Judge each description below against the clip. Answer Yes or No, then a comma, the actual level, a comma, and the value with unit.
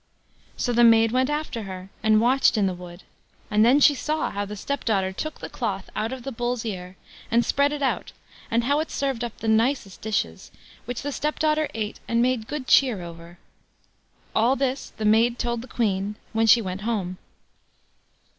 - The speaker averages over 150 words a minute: Yes, average, 190 wpm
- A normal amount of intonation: Yes, average, 4.2 semitones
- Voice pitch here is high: Yes, high, 230 Hz